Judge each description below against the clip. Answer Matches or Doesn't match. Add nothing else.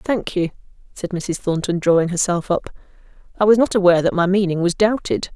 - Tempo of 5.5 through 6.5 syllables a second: Matches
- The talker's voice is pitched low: Doesn't match